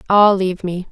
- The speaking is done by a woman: Yes, female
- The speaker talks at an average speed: Yes, average, 195 wpm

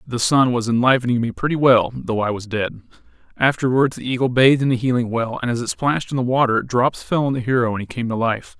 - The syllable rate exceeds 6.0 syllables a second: Yes, 6.2 syllables/s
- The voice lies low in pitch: Yes, low, 125 Hz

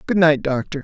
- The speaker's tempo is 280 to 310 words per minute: No, fast, 215 wpm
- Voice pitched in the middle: Yes, medium, 150 Hz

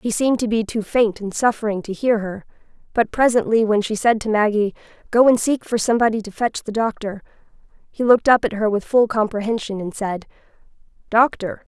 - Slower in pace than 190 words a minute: No, average, 195 wpm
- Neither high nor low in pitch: No, high, 220 Hz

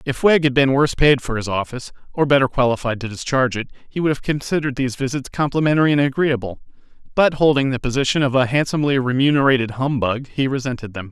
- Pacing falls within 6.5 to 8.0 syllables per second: Yes, 6.8 syllables/s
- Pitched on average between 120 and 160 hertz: Yes, low, 130 Hz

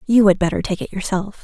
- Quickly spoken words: Yes, fast, 250 wpm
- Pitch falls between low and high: No, high, 195 Hz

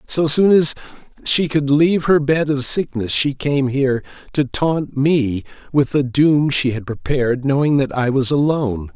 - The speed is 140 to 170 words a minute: No, average, 180 wpm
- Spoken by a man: Yes, male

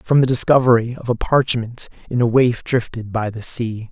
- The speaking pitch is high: No, low, 120 Hz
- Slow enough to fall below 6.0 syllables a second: Yes, 4.9 syllables/s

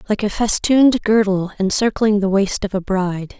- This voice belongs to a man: No, female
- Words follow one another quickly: No, average, 175 wpm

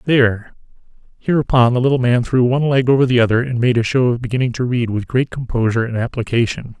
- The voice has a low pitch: Yes, low, 125 Hz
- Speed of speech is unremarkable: No, fast, 210 wpm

